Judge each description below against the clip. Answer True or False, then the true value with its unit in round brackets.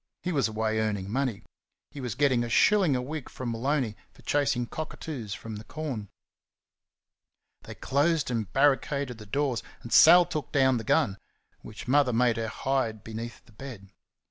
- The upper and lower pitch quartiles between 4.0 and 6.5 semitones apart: True (4.3 semitones)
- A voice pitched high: False (125 Hz)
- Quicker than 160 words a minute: True (170 wpm)